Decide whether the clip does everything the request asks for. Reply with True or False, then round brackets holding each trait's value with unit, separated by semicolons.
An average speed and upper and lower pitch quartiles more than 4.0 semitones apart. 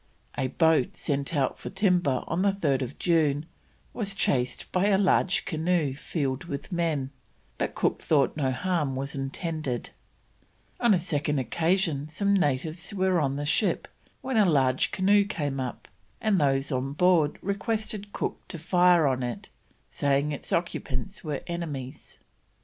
True (150 wpm; 5.1 semitones)